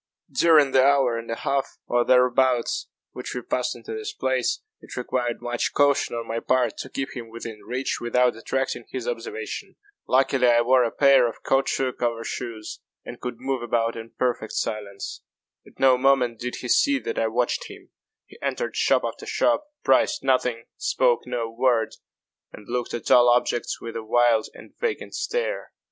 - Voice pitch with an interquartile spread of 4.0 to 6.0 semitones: No, narrow, 2.5 semitones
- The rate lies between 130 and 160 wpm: No, average, 180 wpm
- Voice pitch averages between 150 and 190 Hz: No, low, 125 Hz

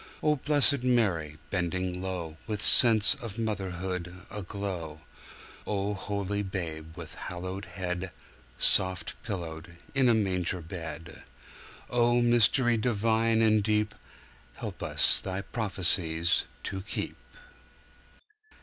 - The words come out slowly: Yes, slow, 90 wpm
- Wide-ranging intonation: No, average, 3.9 semitones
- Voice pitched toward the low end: Yes, very low, 95 Hz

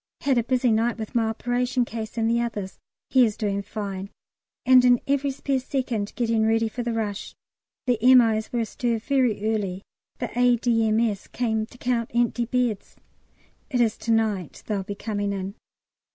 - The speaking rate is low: No, average, 170 wpm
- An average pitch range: No, narrow, 2.3 semitones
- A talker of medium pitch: No, high, 230 Hz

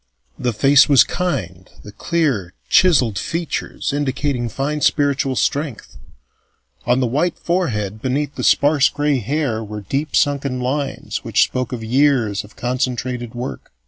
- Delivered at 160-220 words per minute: No, average, 140 wpm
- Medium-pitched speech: No, low, 130 Hz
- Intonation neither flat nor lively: Yes, average, 3.9 semitones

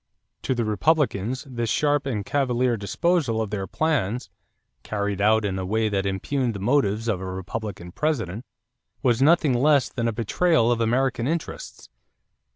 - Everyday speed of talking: Yes, average, 160 wpm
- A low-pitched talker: Yes, low, 115 Hz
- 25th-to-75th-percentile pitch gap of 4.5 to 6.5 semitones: Yes, average, 4.8 semitones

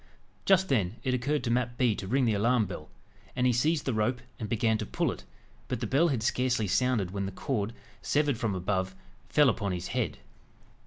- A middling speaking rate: No, fast, 210 wpm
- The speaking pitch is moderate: No, low, 120 Hz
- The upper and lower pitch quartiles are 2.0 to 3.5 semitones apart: No, average, 3.9 semitones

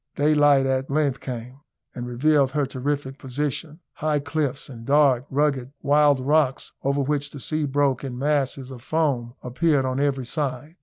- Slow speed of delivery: No, average, 160 wpm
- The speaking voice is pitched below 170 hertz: Yes, medium, 140 Hz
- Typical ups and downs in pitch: No, narrow, 2.2 semitones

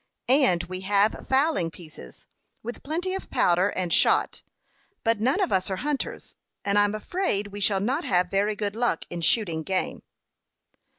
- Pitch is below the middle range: No, high, 205 Hz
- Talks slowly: No, average, 165 wpm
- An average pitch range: No, wide, 5.9 semitones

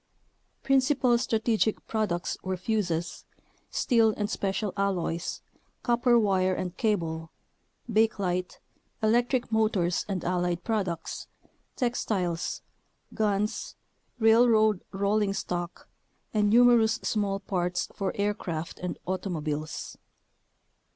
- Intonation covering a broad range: No, average, 3.7 semitones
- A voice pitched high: Yes, high, 200 Hz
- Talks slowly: Yes, slow, 95 wpm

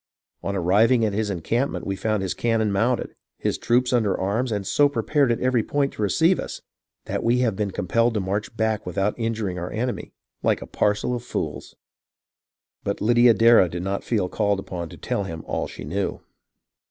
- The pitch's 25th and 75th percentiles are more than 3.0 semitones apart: Yes, average, 3.4 semitones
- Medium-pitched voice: No, low, 110 Hz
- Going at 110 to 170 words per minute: No, average, 190 wpm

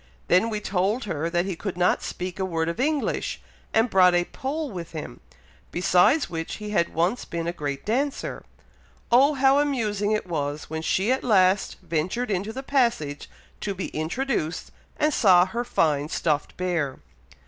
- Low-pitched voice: No, medium, 185 Hz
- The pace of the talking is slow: No, average, 170 wpm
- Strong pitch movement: Yes, wide, 5.9 semitones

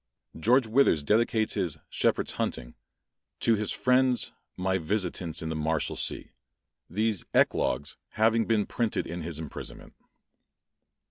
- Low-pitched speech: Yes, low, 100 Hz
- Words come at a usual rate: No, slow, 120 wpm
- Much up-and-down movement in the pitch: Yes, wide, 5.8 semitones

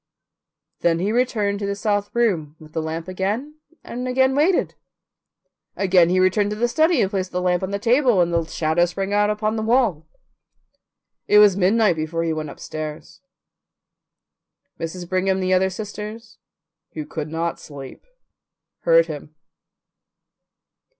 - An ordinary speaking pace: Yes, average, 150 wpm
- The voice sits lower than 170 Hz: No, high, 190 Hz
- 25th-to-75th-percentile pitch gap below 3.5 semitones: No, average, 4.4 semitones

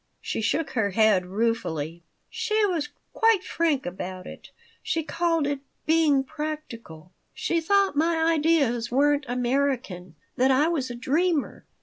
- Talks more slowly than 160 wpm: Yes, slow, 135 wpm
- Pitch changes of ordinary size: No, wide, 6.1 semitones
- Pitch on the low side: No, very high, 280 Hz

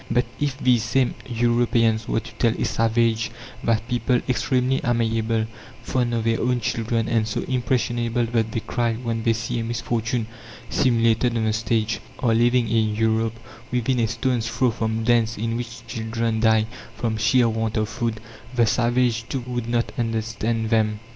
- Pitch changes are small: Yes, narrow, 1.3 semitones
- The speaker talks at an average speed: Yes, average, 170 wpm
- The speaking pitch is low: Yes, low, 115 Hz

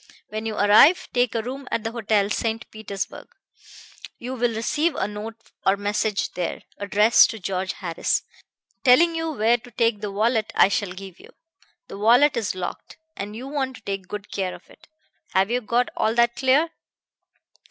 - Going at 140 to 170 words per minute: No, average, 180 wpm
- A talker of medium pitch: No, high, 220 Hz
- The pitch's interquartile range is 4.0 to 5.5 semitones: No, average, 3.4 semitones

